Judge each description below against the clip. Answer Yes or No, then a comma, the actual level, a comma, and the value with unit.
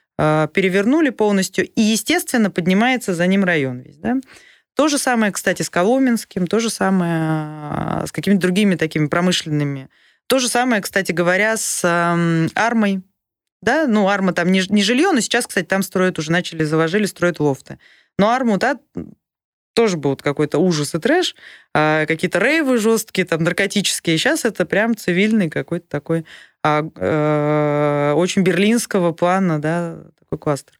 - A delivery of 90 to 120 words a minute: No, average, 145 wpm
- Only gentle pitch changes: No, average, 5.2 semitones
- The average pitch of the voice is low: No, medium, 185 Hz